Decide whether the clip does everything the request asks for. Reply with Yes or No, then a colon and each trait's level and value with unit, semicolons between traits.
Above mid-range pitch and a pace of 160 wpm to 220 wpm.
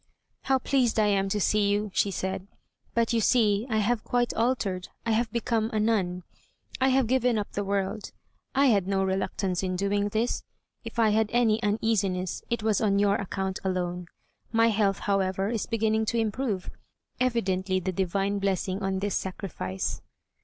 Yes: high, 205 Hz; average, 175 wpm